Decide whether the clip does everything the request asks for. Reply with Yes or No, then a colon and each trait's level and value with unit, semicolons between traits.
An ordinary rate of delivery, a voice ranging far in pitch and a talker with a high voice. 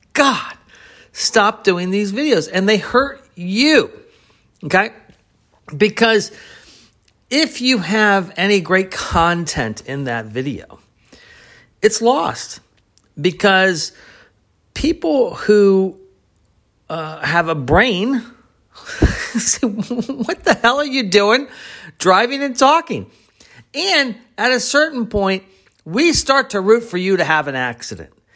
No: slow, 115 wpm; wide, 6.4 semitones; high, 210 Hz